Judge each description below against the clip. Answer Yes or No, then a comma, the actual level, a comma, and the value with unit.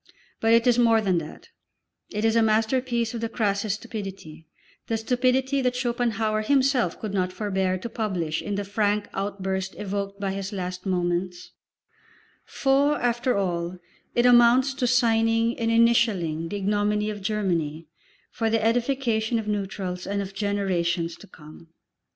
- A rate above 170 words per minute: No, average, 150 wpm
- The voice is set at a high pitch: Yes, high, 210 Hz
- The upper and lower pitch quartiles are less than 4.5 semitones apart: Yes, average, 3.5 semitones